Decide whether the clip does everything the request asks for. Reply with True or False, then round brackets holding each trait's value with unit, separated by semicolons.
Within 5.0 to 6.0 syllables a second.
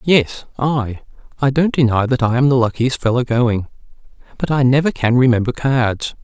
False (4.7 syllables/s)